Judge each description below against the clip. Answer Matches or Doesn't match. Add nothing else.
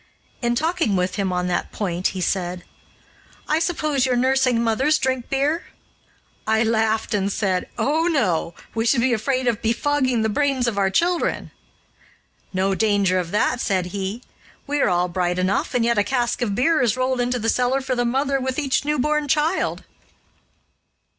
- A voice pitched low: Doesn't match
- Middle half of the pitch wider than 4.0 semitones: Matches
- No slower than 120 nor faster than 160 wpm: Doesn't match